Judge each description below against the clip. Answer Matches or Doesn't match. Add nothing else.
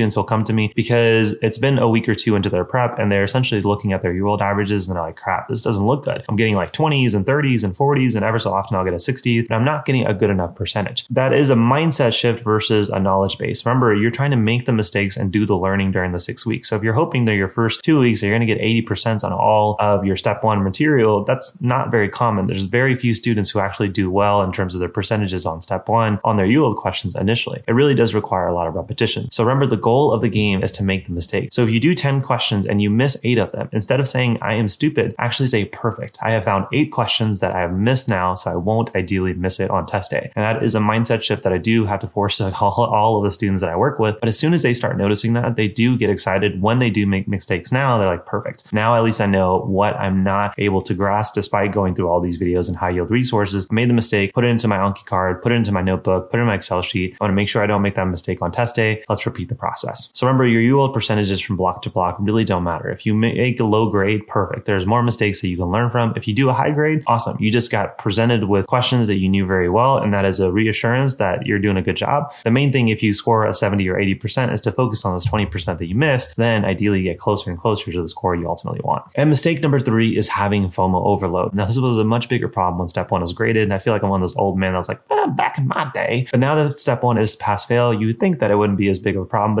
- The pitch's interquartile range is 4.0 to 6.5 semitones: Doesn't match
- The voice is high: Doesn't match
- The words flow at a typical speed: Doesn't match